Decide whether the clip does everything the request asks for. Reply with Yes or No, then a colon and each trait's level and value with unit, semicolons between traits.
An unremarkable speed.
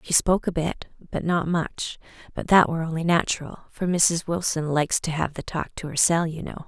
No: fast, 215 wpm